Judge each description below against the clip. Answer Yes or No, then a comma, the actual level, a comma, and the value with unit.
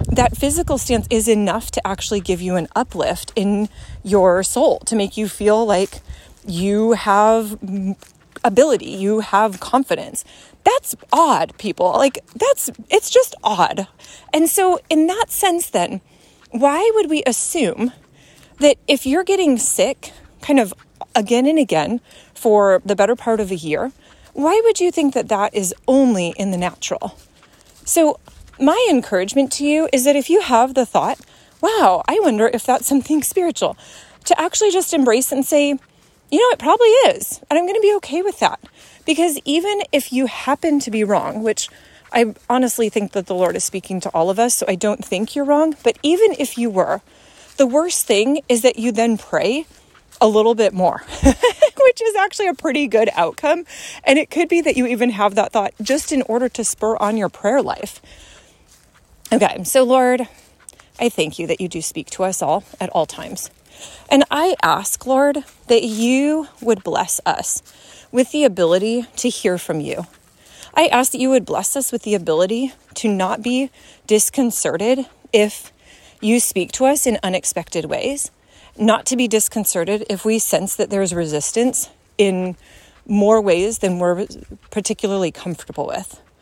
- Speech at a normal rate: Yes, average, 175 wpm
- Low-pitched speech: No, high, 240 Hz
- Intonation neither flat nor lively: No, wide, 5.8 semitones